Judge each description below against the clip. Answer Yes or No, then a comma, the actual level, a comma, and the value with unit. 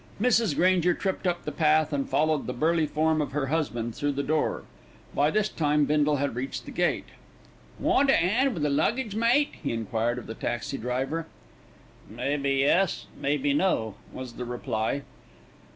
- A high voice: No, medium, 150 Hz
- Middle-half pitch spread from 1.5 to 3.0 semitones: No, average, 4.6 semitones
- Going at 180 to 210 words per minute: No, average, 170 wpm